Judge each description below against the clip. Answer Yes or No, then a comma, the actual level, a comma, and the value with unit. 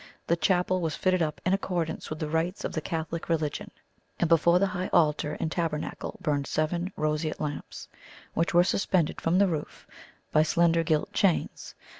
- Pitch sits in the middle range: Yes, medium, 165 Hz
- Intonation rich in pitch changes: No, narrow, 2.4 semitones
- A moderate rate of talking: Yes, average, 175 wpm